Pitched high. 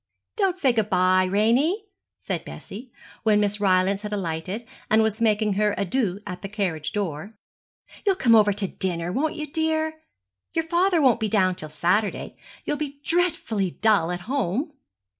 Yes: high, 210 Hz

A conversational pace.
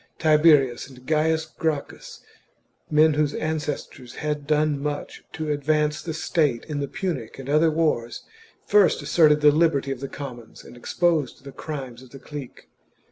Yes: average, 165 wpm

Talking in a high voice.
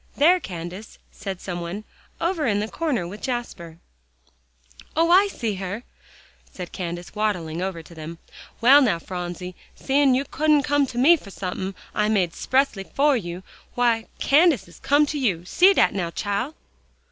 Yes: high, 210 Hz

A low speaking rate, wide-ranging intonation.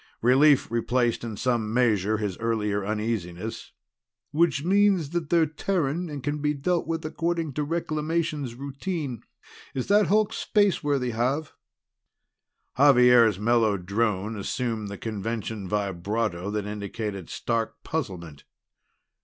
Yes: slow, 120 wpm; wide, 6.2 semitones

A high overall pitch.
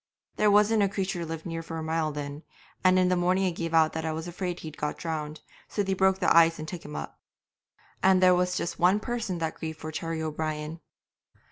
No: medium, 165 Hz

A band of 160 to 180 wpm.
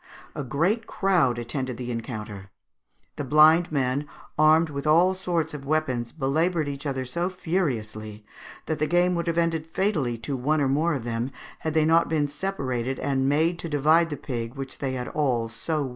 No: average, 190 wpm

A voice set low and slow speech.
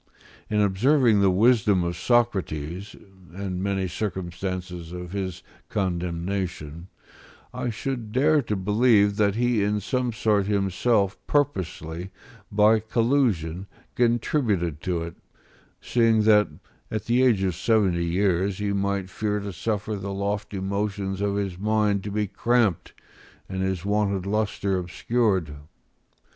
Yes: low, 100 Hz; slow, 125 wpm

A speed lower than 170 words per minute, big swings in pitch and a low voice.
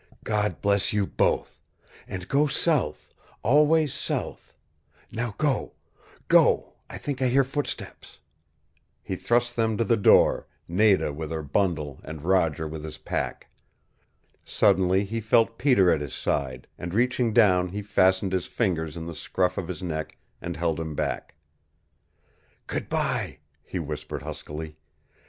Yes: average, 145 wpm; wide, 6.3 semitones; very low, 95 Hz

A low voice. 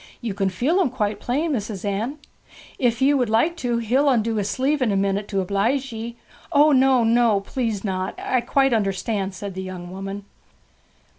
No: high, 225 Hz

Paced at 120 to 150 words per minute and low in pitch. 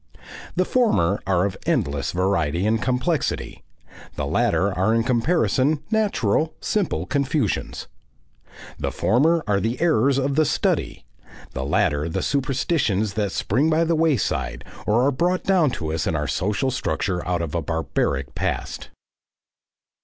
Yes: average, 145 wpm; low, 115 Hz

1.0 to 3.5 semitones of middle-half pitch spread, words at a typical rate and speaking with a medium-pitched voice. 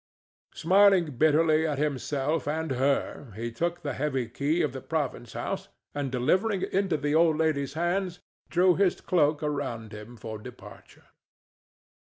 No: average, 4.1 semitones; average, 150 wpm; medium, 150 Hz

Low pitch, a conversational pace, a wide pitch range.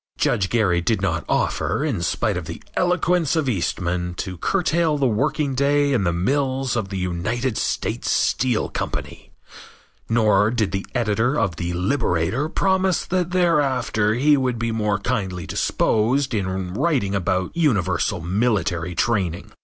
Yes: low, 110 Hz; average, 145 wpm; wide, 7.0 semitones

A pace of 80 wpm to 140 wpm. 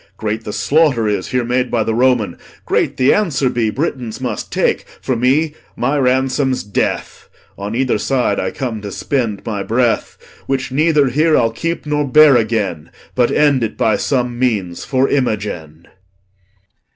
No: average, 165 wpm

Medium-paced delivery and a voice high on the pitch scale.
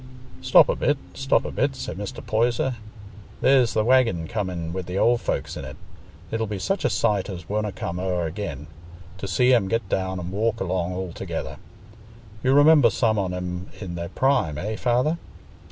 No: average, 185 wpm; low, 105 Hz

